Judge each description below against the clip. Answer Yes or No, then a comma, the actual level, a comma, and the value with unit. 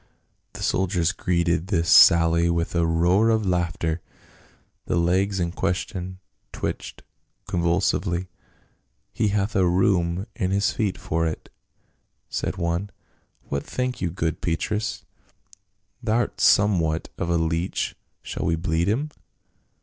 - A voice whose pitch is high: No, very low, 90 Hz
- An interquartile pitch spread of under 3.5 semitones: Yes, average, 2.8 semitones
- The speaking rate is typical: No, slow, 130 wpm